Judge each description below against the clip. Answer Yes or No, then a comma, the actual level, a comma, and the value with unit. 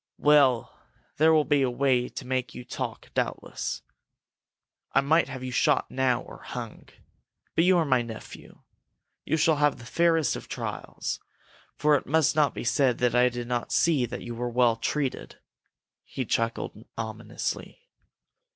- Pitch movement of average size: Yes, average, 3.6 semitones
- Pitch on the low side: Yes, low, 130 Hz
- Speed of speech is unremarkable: Yes, average, 160 wpm